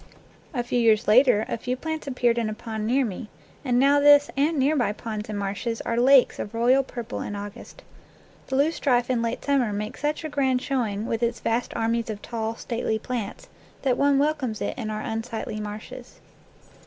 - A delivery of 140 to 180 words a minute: No, average, 200 wpm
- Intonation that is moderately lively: Yes, average, 3.7 semitones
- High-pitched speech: Yes, high, 240 Hz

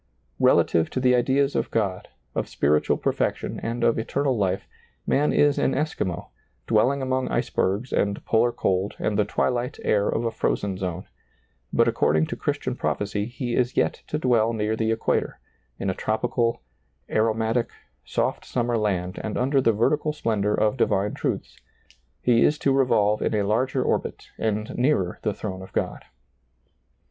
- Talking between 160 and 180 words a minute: Yes, average, 165 wpm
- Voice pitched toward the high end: No, low, 115 Hz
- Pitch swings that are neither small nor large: Yes, average, 3.6 semitones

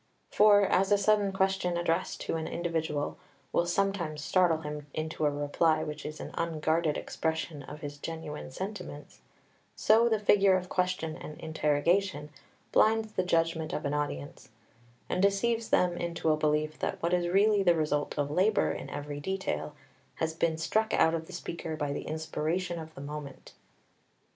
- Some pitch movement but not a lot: Yes, average, 3.8 semitones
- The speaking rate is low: No, average, 170 wpm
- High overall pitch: No, medium, 165 Hz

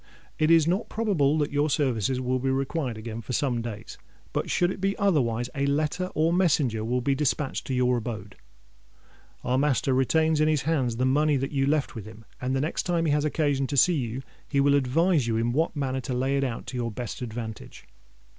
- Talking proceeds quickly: Yes, fast, 220 wpm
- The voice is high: No, low, 135 Hz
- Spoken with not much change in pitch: No, average, 3.6 semitones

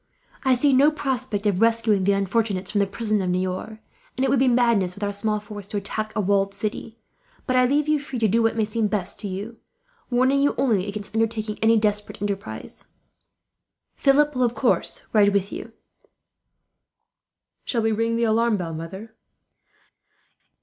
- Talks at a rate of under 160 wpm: No, average, 180 wpm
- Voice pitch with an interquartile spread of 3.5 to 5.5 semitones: No, average, 2.9 semitones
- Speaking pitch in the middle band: No, high, 220 Hz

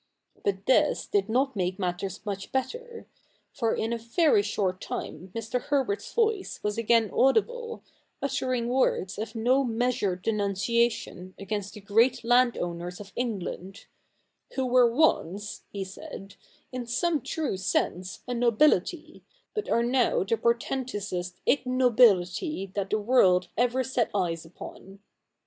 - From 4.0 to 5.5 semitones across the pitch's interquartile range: Yes, average, 4.8 semitones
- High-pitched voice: Yes, high, 230 Hz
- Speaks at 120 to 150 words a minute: Yes, average, 140 wpm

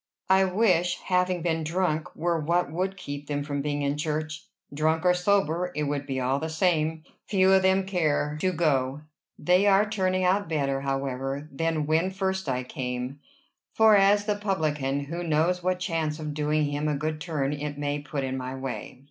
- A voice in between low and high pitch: Yes, medium, 155 Hz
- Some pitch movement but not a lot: Yes, average, 4.1 semitones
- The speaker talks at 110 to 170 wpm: No, average, 190 wpm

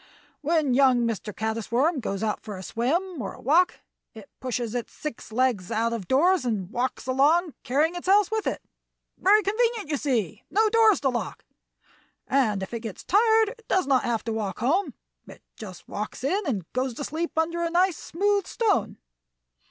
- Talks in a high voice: Yes, very high, 270 Hz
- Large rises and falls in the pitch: Yes, wide, 8.0 semitones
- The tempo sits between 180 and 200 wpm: Yes, average, 190 wpm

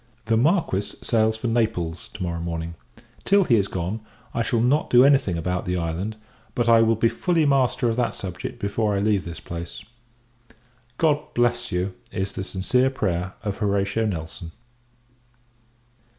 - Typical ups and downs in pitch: Yes, average, 4.9 semitones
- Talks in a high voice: No, low, 105 Hz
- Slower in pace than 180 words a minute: Yes, average, 165 wpm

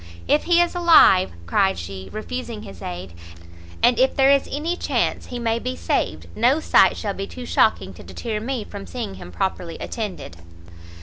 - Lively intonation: Yes, wide, 8.0 semitones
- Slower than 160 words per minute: No, average, 180 wpm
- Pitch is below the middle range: No, high, 220 Hz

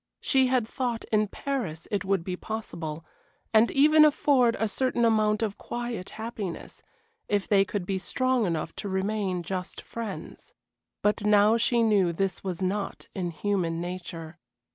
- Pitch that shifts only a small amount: No, average, 4.1 semitones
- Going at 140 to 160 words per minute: Yes, average, 155 wpm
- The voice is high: Yes, high, 205 Hz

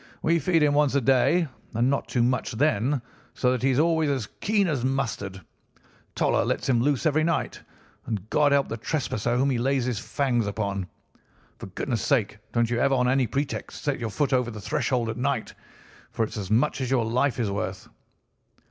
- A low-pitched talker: Yes, low, 130 Hz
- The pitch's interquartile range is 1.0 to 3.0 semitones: No, average, 3.7 semitones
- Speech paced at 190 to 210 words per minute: Yes, average, 200 wpm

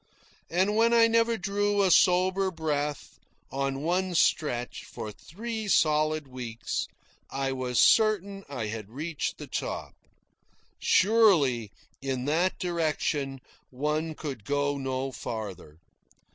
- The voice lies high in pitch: No, medium, 155 Hz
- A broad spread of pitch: Yes, wide, 6.0 semitones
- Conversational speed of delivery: No, slow, 115 wpm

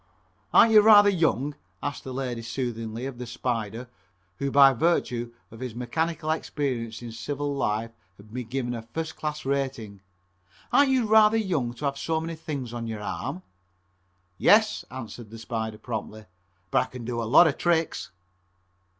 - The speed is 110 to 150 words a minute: No, average, 165 wpm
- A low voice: Yes, low, 130 Hz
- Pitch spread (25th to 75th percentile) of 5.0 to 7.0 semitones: Yes, wide, 5.5 semitones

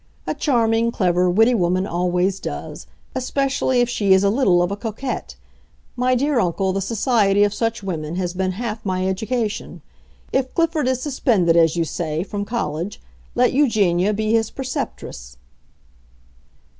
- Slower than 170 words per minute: Yes, average, 150 wpm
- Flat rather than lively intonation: No, average, 5.2 semitones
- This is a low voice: No, high, 205 Hz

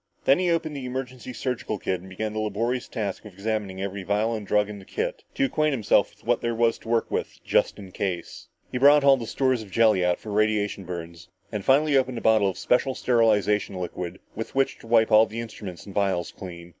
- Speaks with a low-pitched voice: Yes, low, 110 Hz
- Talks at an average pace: No, fast, 230 wpm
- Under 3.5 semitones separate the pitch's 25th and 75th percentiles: No, average, 4.3 semitones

